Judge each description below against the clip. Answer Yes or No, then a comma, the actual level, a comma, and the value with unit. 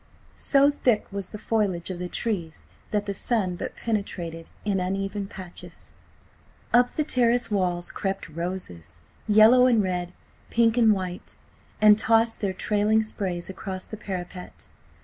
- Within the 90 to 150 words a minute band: Yes, average, 145 wpm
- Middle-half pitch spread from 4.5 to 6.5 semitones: No, average, 3.6 semitones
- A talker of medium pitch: No, high, 200 Hz